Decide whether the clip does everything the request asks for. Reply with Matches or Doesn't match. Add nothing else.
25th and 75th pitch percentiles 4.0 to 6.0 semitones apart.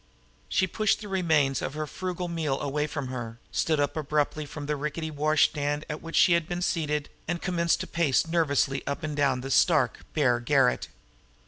Doesn't match